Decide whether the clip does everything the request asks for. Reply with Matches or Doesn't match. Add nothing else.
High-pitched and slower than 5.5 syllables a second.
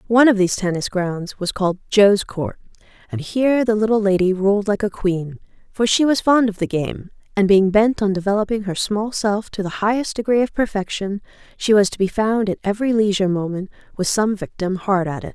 Doesn't match